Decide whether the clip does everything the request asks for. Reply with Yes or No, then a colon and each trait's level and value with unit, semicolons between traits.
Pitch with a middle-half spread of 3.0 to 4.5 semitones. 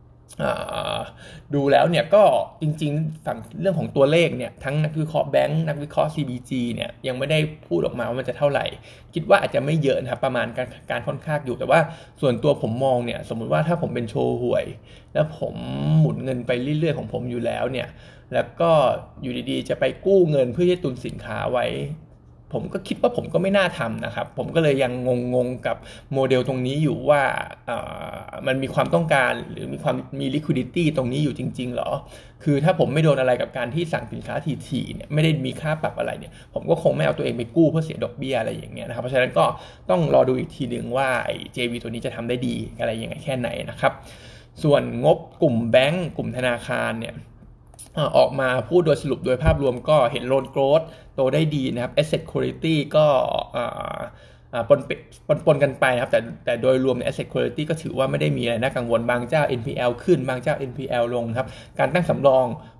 Yes: average, 3.9 semitones